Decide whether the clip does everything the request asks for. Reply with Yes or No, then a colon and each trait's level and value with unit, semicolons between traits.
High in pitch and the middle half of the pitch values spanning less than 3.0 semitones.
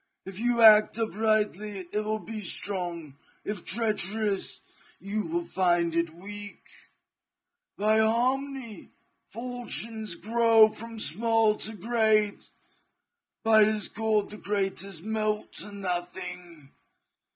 Yes: high, 215 Hz; narrow, 2.5 semitones